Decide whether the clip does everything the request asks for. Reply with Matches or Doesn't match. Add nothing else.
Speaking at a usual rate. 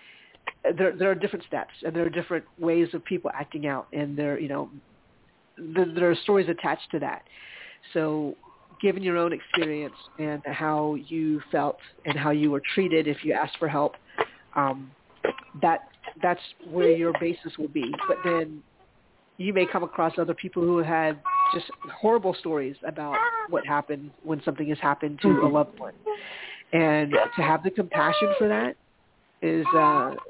Matches